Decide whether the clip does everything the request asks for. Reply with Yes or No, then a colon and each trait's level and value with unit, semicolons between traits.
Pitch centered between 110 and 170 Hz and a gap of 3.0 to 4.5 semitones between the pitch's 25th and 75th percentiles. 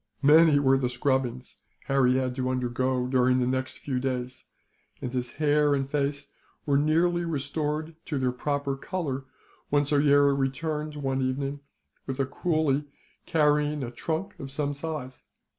No: medium, 140 Hz; narrow, 2.4 semitones